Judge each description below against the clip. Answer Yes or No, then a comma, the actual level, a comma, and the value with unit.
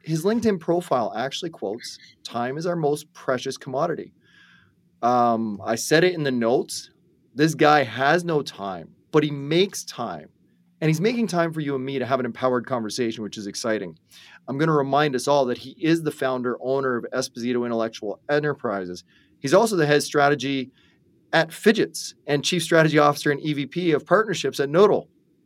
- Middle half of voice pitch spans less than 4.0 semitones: No, average, 4.3 semitones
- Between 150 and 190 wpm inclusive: Yes, average, 180 wpm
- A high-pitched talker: No, medium, 140 Hz